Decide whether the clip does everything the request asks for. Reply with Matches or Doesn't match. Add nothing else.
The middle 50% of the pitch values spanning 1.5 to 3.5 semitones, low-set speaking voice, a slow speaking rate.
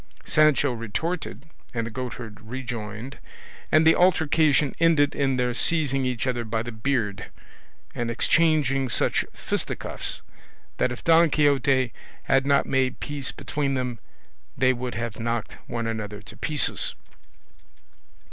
Doesn't match